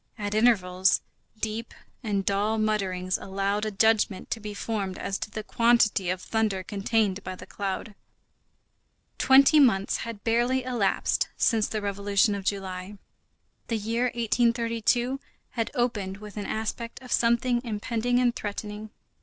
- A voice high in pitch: Yes, high, 215 Hz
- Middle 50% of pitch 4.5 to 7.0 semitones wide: No, average, 2.7 semitones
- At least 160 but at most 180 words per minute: No, average, 140 wpm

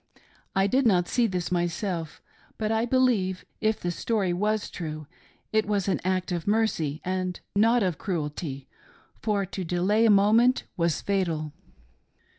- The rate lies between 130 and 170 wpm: Yes, average, 150 wpm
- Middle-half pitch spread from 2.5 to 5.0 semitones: Yes, average, 3.7 semitones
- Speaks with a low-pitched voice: No, high, 190 Hz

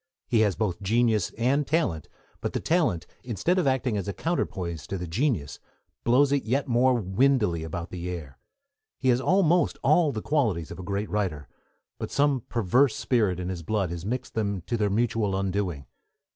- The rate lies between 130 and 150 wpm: No, average, 185 wpm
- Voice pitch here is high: No, low, 110 Hz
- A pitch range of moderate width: No, wide, 6.3 semitones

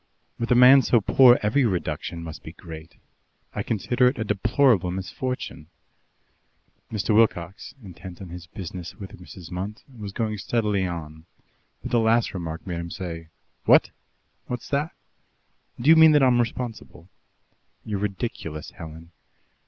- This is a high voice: No, low, 100 Hz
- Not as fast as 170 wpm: Yes, average, 145 wpm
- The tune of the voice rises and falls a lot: Yes, wide, 5.7 semitones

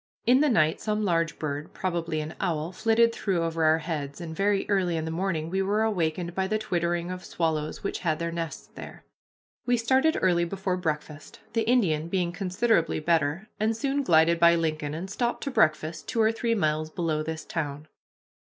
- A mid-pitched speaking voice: Yes, medium, 170 Hz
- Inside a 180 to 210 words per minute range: Yes, average, 190 wpm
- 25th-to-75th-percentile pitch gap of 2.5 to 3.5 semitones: No, average, 4.5 semitones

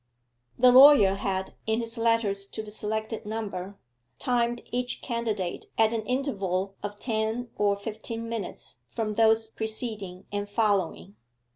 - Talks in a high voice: Yes, high, 220 Hz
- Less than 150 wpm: Yes, slow, 135 wpm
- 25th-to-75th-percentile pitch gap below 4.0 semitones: Yes, narrow, 2.5 semitones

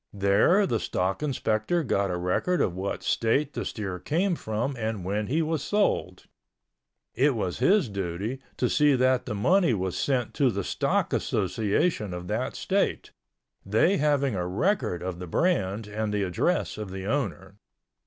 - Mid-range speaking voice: No, low, 110 Hz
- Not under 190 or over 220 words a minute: No, average, 165 wpm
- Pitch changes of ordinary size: No, wide, 7.3 semitones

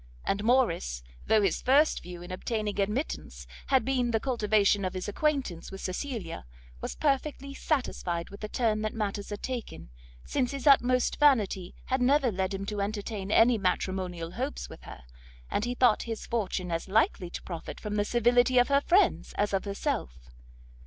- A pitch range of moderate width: Yes, average, 4.9 semitones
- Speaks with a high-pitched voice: Yes, high, 210 Hz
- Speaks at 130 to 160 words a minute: No, average, 175 wpm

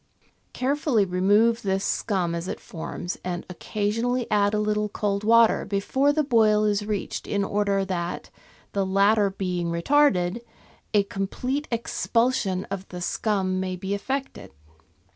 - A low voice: No, high, 205 Hz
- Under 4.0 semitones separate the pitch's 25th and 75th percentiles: Yes, average, 3.4 semitones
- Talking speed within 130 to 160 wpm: Yes, average, 140 wpm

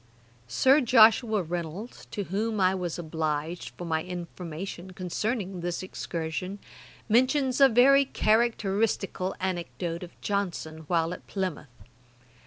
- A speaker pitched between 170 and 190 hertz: Yes, medium, 185 Hz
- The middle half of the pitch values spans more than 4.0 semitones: Yes, average, 4.5 semitones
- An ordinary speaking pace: No, slow, 120 wpm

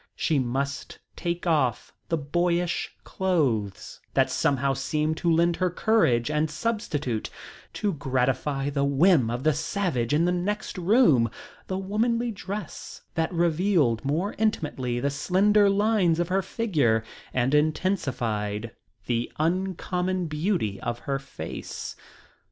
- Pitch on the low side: No, medium, 160 Hz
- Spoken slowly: Yes, slow, 130 wpm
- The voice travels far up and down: Yes, wide, 5.8 semitones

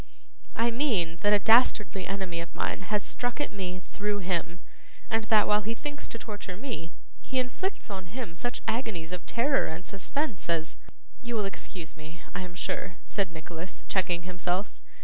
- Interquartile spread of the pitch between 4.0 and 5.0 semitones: Yes, average, 4.6 semitones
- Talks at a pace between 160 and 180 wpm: Yes, average, 175 wpm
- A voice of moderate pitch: No, high, 195 Hz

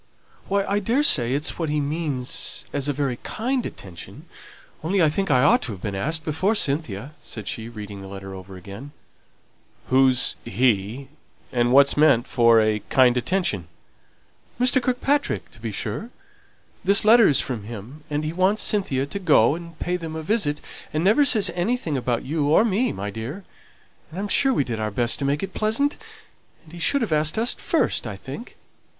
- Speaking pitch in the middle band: Yes, medium, 145 Hz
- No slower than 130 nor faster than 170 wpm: No, average, 185 wpm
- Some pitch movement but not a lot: No, wide, 8.3 semitones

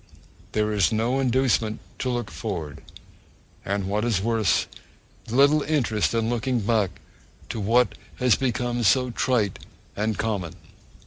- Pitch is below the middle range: Yes, low, 115 Hz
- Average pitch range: Yes, average, 3.1 semitones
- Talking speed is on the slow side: Yes, slow, 130 wpm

